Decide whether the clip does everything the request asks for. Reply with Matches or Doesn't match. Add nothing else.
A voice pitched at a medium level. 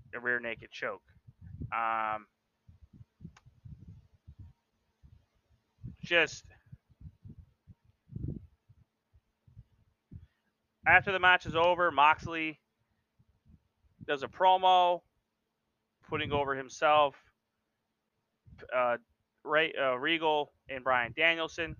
Doesn't match